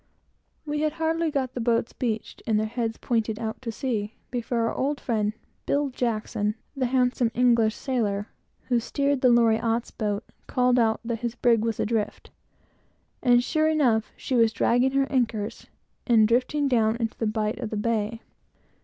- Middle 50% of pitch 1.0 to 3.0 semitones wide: Yes, narrow, 2.6 semitones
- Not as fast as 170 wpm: Yes, average, 160 wpm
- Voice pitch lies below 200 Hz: No, high, 235 Hz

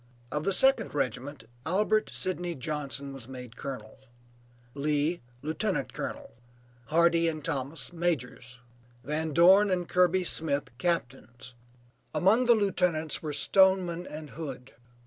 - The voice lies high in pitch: No, medium, 160 Hz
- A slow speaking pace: Yes, slow, 120 wpm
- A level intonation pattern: No, average, 4.6 semitones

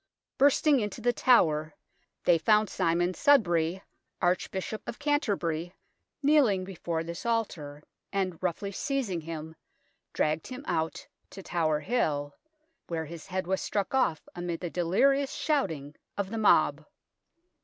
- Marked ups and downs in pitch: Yes, wide, 5.8 semitones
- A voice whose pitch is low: No, medium, 185 Hz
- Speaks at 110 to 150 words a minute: Yes, slow, 135 wpm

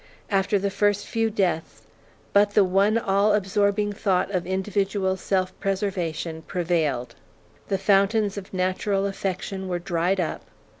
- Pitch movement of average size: No, narrow, 1.8 semitones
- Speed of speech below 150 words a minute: Yes, slow, 135 wpm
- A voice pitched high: Yes, high, 195 Hz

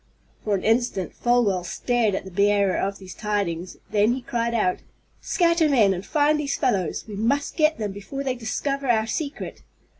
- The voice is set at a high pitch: Yes, high, 225 Hz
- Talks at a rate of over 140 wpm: Yes, average, 180 wpm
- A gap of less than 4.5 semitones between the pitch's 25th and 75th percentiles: No, average, 5.3 semitones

